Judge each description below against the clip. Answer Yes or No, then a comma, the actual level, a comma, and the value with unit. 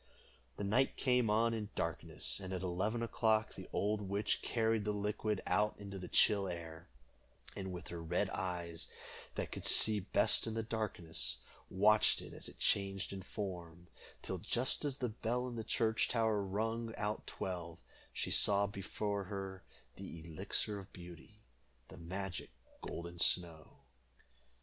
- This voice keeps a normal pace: Yes, average, 155 wpm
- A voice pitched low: Yes, low, 100 Hz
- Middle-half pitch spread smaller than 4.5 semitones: Yes, average, 3.5 semitones